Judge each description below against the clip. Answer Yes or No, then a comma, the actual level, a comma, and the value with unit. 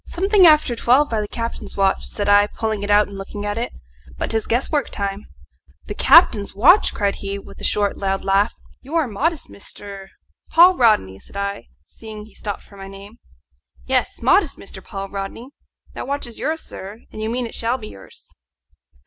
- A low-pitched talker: No, high, 210 Hz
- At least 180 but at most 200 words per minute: Yes, average, 195 wpm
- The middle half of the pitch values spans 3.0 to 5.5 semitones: Yes, average, 3.7 semitones